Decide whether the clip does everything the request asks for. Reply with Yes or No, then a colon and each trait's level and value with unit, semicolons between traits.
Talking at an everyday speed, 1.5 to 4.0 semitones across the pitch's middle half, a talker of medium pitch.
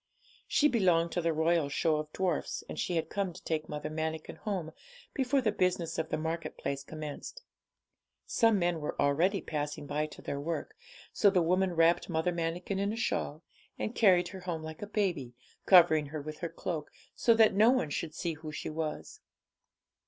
Yes: average, 190 wpm; average, 3.5 semitones; medium, 170 Hz